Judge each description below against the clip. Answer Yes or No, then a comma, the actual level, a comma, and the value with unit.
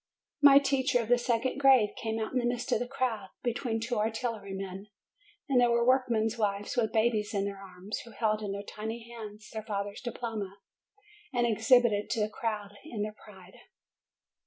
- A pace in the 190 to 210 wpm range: Yes, average, 195 wpm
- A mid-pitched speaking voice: No, high, 220 Hz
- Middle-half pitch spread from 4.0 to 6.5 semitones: No, average, 2.7 semitones